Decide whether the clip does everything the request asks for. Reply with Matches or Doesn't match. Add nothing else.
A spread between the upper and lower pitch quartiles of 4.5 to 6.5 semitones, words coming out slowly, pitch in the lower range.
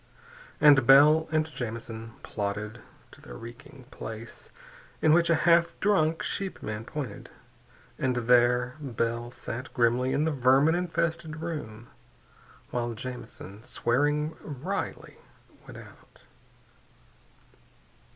Matches